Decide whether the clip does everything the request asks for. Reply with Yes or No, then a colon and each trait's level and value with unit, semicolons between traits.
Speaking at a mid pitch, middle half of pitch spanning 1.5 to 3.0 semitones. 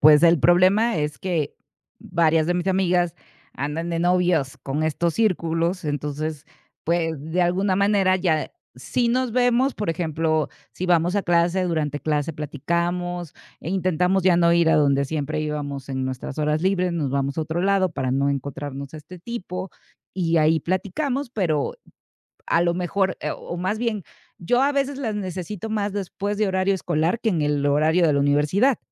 No: medium, 170 Hz; average, 3.8 semitones